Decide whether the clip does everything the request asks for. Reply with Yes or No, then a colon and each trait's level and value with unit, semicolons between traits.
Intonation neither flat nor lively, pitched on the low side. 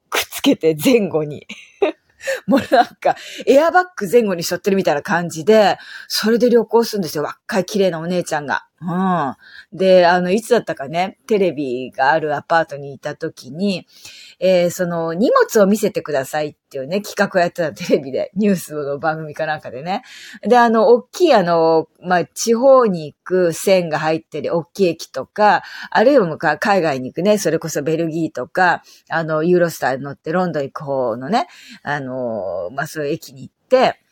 No: average, 4.6 semitones; medium, 175 Hz